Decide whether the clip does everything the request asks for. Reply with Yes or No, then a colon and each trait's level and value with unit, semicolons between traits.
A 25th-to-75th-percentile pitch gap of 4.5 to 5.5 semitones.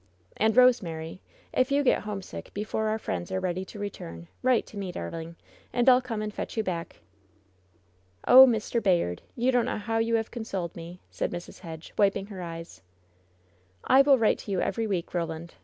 Yes: average, 5.1 semitones